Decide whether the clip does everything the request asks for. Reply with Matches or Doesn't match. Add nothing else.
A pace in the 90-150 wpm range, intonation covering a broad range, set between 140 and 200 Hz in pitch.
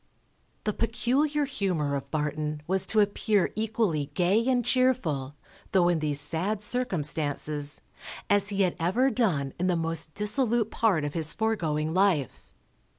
Matches